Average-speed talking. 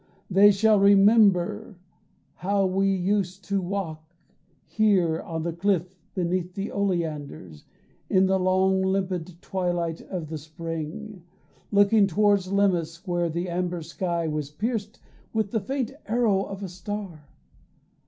No: slow, 130 wpm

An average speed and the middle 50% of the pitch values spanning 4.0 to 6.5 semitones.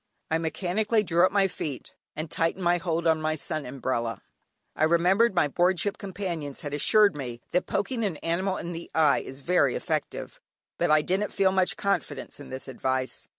Yes: average, 190 wpm; average, 4.4 semitones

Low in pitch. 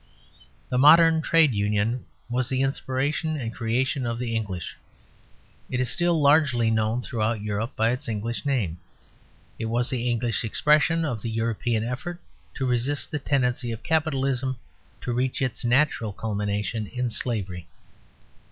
Yes: low, 120 Hz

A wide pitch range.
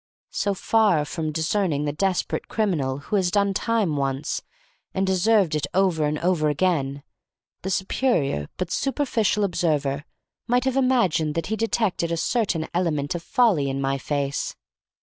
Yes: wide, 5.7 semitones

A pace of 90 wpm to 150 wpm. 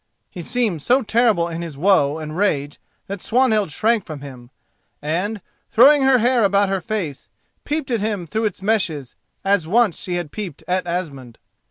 No: average, 175 wpm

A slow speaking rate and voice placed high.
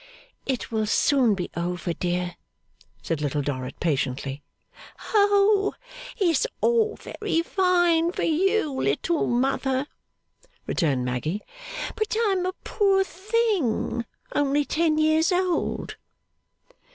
Yes: slow, 105 wpm; very high, 305 Hz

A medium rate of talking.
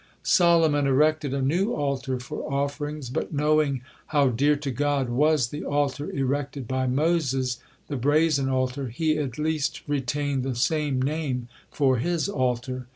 Yes: average, 150 wpm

